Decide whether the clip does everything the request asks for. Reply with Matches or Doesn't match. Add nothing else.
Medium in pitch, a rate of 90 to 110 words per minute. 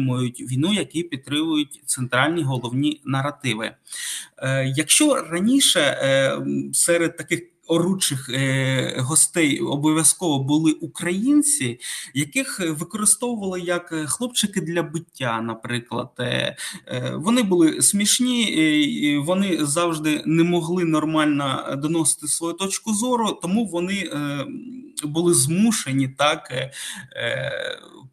Matches